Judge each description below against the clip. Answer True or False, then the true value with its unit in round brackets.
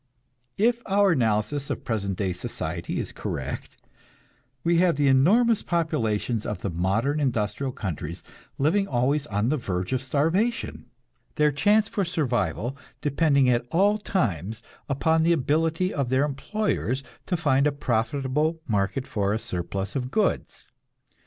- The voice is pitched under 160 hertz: True (135 Hz)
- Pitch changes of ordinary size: False (7.1 semitones)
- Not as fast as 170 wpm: True (140 wpm)